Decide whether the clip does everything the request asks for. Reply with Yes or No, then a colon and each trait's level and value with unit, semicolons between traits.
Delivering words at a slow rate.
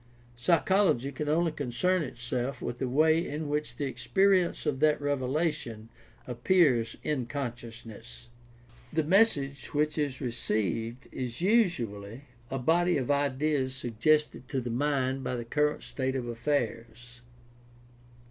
Yes: slow, 130 wpm